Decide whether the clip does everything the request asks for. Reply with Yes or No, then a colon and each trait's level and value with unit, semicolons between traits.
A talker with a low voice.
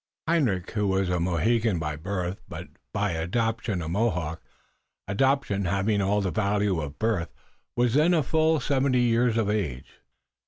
Yes: low, 105 Hz